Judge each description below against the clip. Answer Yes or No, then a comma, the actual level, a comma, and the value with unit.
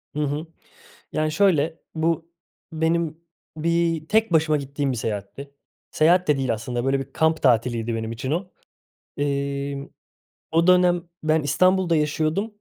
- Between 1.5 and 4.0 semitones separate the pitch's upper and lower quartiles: Yes, average, 3.4 semitones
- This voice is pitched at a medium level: Yes, medium, 155 Hz